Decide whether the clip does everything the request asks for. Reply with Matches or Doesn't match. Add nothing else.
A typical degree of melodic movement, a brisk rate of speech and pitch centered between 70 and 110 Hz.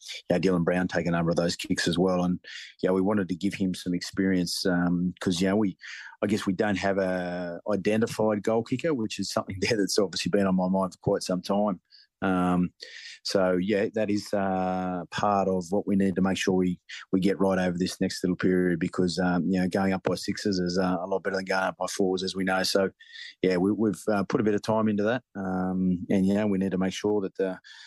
Doesn't match